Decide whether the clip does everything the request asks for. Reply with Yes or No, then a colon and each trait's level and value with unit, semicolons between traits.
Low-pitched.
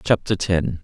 Yes: very low, 95 Hz